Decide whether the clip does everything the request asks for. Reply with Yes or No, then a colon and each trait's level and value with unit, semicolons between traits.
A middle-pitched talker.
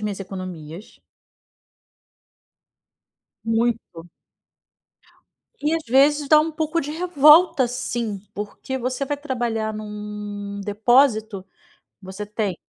No: high, 225 Hz